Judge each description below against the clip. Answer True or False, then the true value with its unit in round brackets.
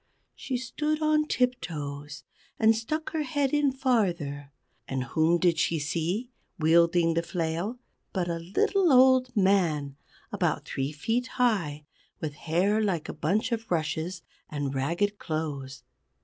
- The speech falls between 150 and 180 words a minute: False (135 wpm)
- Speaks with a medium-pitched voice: True (175 Hz)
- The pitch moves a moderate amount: False (8.0 semitones)